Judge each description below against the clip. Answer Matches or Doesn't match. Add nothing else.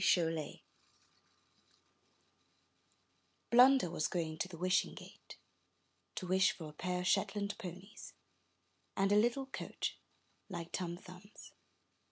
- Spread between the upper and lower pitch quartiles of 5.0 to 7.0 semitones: Doesn't match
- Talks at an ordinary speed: Doesn't match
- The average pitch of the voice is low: Doesn't match